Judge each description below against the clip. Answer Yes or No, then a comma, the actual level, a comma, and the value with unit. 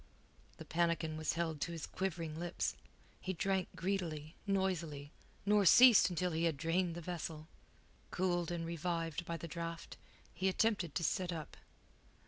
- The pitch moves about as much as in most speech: No, narrow, 2.1 semitones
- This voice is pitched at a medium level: Yes, medium, 170 Hz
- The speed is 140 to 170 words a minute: Yes, average, 150 wpm